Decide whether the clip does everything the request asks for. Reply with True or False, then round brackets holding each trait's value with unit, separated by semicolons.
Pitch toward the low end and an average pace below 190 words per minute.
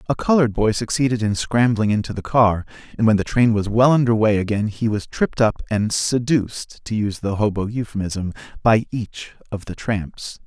False (110 Hz; 195 wpm)